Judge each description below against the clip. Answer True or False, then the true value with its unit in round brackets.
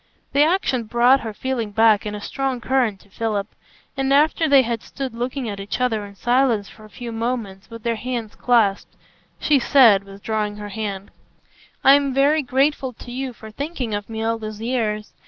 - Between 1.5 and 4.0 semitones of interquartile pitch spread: True (3.7 semitones)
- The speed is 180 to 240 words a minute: True (190 wpm)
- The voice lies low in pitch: False (230 Hz)